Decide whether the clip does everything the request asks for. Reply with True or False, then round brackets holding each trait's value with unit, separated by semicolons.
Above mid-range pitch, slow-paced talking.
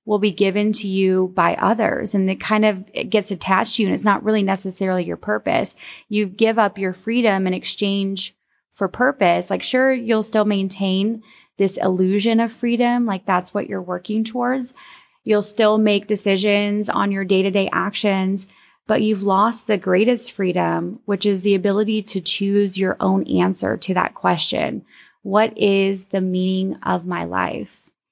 False (200 Hz; 175 wpm)